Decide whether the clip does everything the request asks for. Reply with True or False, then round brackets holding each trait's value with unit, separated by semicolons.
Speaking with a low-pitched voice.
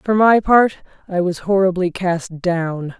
False (185 Hz)